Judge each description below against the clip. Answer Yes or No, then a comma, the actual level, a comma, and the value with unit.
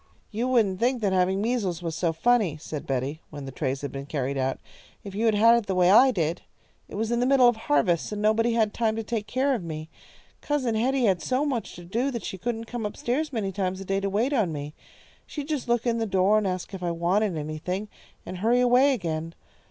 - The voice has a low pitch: No, high, 205 Hz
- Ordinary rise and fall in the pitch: No, wide, 5.7 semitones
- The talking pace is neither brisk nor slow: No, fast, 245 wpm